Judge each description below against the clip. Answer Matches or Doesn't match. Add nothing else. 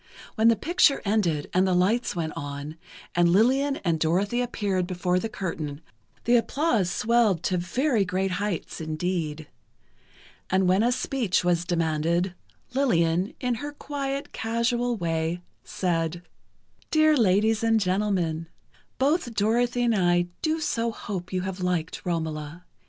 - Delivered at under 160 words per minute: Matches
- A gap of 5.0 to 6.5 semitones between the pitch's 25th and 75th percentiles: Matches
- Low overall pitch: Doesn't match